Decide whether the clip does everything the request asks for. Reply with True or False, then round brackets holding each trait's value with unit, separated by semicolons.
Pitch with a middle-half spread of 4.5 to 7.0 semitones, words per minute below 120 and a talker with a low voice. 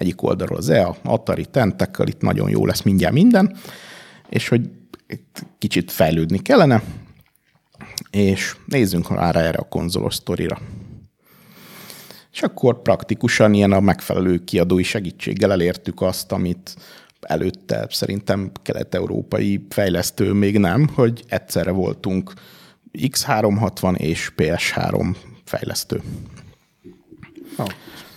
True (4.8 semitones; 105 wpm; 100 Hz)